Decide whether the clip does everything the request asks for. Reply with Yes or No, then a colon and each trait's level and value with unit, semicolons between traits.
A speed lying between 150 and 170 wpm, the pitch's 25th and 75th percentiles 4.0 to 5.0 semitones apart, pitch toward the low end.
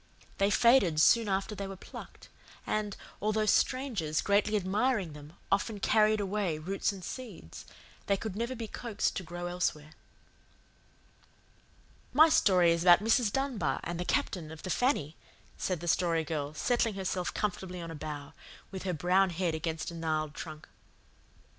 No: average, 160 wpm; average, 4.5 semitones; medium, 185 Hz